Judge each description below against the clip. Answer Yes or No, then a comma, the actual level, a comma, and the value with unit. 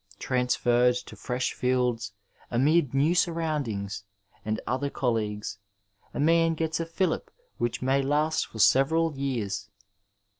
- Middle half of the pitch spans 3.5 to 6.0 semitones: Yes, average, 4.8 semitones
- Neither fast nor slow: No, slow, 120 wpm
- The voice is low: Yes, low, 130 Hz